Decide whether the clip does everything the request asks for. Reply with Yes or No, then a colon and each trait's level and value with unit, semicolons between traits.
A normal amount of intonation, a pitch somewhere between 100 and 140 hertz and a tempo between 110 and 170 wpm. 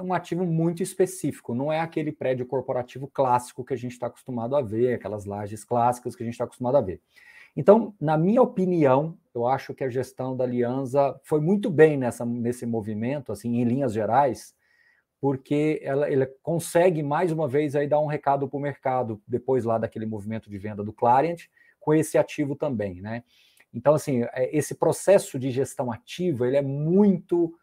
No: average, 4.4 semitones; low, 135 Hz; fast, 185 wpm